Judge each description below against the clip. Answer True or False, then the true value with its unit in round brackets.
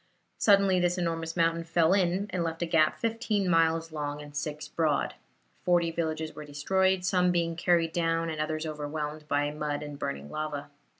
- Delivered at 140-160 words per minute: False (175 wpm)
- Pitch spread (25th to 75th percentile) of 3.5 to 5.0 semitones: False (2.7 semitones)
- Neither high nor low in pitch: True (165 Hz)